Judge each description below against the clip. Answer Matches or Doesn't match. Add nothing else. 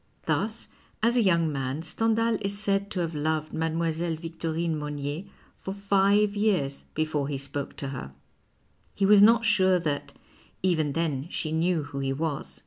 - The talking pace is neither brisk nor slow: Matches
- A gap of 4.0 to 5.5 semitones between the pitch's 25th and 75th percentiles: Matches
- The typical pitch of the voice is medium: Matches